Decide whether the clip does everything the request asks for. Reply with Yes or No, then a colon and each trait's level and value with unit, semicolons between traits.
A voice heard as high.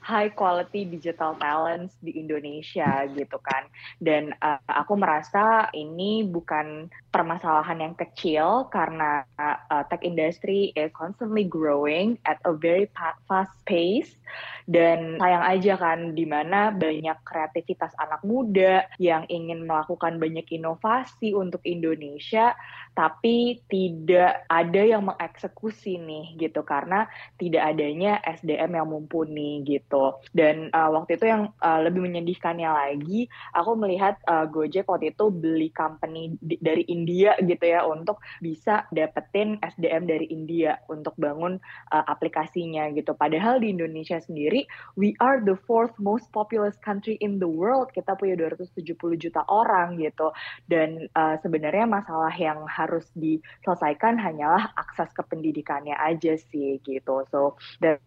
No: medium, 165 Hz